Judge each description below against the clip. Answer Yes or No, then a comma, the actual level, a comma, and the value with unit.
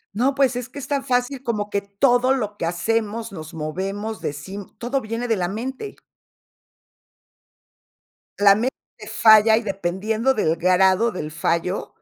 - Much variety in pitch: No, average, 4.4 semitones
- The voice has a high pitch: Yes, high, 215 Hz